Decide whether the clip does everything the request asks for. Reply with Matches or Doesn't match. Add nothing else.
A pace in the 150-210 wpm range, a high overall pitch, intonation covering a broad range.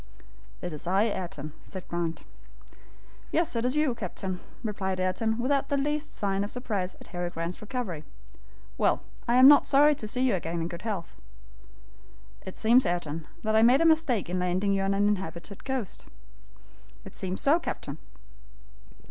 Matches